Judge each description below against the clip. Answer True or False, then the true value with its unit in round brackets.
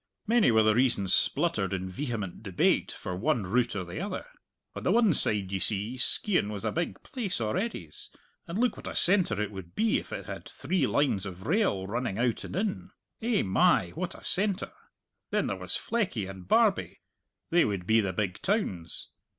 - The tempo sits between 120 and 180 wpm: False (190 wpm)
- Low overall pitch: True (115 Hz)